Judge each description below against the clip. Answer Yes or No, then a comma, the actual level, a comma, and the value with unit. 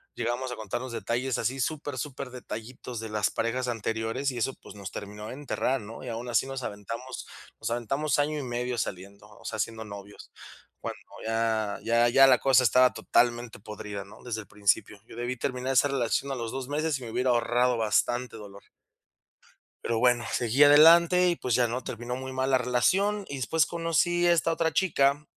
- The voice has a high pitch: No, low, 125 Hz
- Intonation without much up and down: No, average, 3.2 semitones